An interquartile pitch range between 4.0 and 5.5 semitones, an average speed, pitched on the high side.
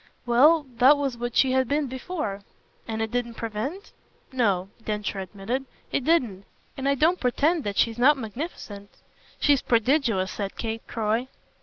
Yes: average, 4.6 semitones; average, 155 wpm; high, 240 Hz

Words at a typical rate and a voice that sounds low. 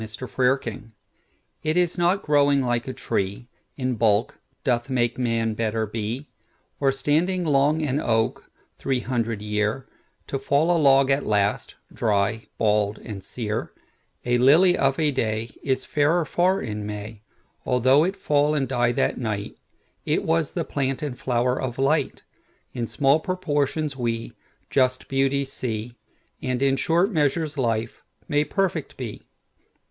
No: slow, 130 wpm; low, 130 Hz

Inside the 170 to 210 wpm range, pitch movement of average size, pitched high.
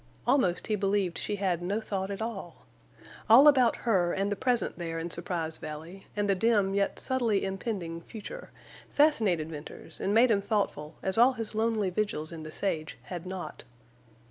Yes: average, 175 wpm; average, 4.3 semitones; high, 195 Hz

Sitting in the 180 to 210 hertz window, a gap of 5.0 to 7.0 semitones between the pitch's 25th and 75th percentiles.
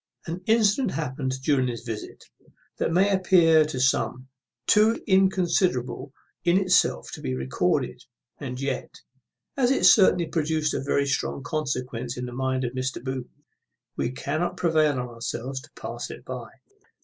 No: medium, 140 Hz; wide, 5.4 semitones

